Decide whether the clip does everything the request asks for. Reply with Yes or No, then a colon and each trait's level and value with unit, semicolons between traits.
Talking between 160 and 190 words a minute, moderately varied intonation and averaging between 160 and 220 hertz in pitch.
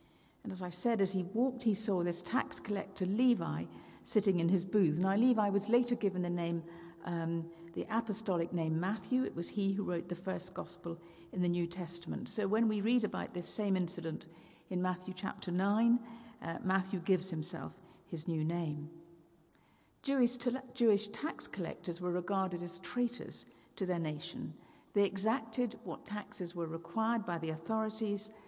Yes: average, 170 wpm; average, 4.2 semitones; high, 190 Hz